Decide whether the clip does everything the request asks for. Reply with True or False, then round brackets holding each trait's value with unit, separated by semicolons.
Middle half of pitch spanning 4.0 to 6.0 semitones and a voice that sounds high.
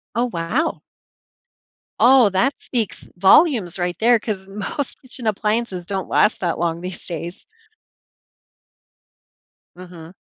True (5.1 semitones; 195 Hz)